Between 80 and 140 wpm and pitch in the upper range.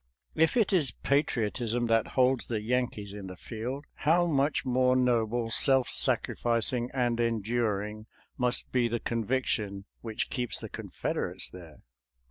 No: slow, 135 wpm; low, 120 Hz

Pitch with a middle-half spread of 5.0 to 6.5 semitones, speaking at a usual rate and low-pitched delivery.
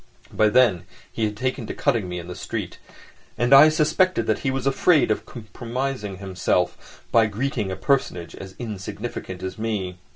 Yes: wide, 5.6 semitones; average, 170 wpm; low, 110 Hz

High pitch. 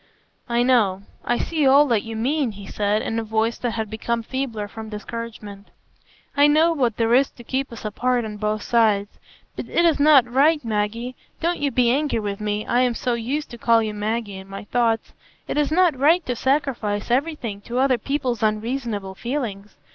Yes: high, 235 Hz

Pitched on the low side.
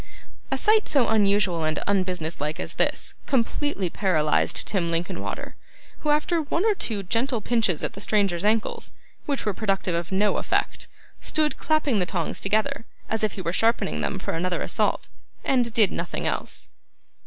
No: high, 205 Hz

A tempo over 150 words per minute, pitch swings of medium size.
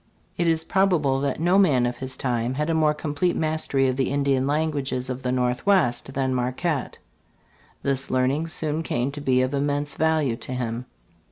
Yes: average, 180 wpm; average, 3.5 semitones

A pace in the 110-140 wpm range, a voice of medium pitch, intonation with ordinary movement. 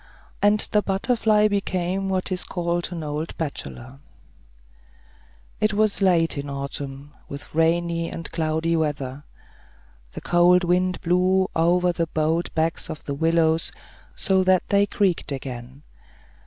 Yes: slow, 135 wpm; medium, 170 Hz; average, 3.2 semitones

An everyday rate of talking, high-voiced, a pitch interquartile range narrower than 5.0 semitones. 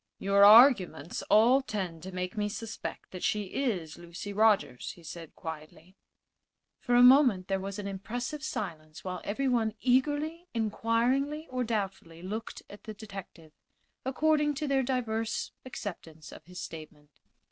No: average, 145 wpm; high, 210 Hz; wide, 5.6 semitones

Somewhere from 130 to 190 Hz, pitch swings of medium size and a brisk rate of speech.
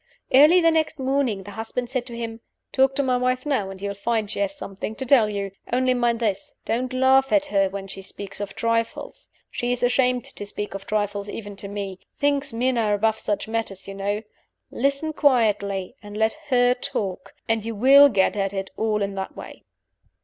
No: high, 225 Hz; average, 4.1 semitones; fast, 210 wpm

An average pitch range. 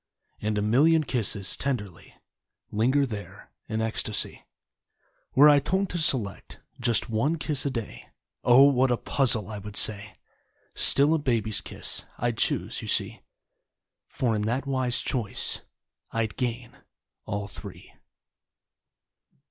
Yes: average, 4.4 semitones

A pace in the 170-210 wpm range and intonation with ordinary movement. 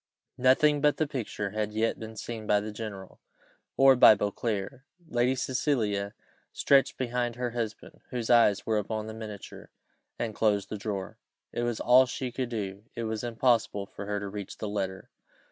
Yes: average, 175 wpm; average, 3.0 semitones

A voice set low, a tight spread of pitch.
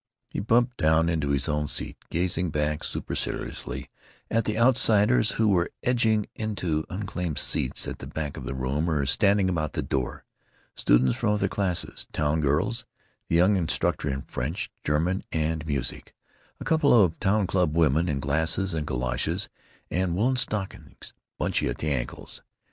No: very low, 85 Hz; wide, 5.4 semitones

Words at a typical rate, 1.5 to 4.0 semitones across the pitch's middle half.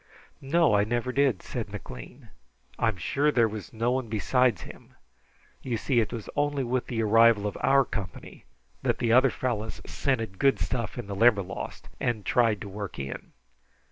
Yes: average, 175 wpm; average, 3.6 semitones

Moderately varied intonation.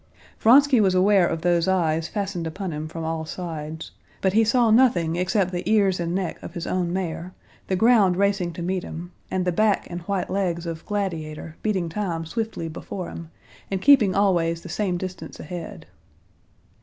Yes: average, 3.1 semitones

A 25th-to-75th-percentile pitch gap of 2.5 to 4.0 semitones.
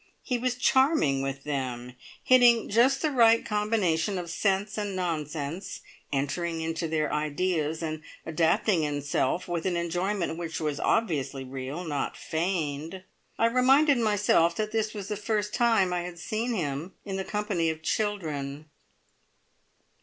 No: wide, 5.5 semitones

